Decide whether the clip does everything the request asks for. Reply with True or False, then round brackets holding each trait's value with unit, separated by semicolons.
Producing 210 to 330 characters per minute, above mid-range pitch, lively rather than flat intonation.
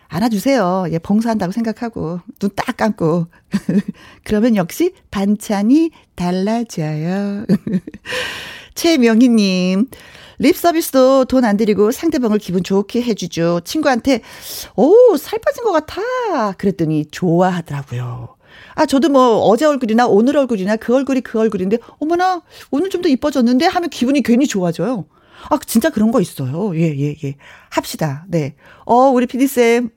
True (295 characters per minute; 225 Hz; 6.5 semitones)